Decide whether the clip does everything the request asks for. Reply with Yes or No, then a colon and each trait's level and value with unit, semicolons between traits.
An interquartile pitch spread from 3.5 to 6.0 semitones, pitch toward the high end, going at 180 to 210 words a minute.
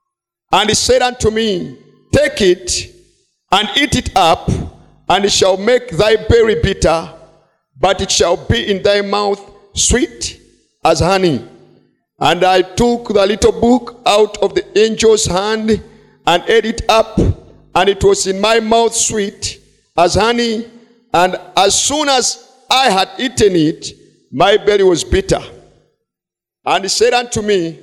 No: average, 4.3 semitones; high, 215 Hz; average, 150 wpm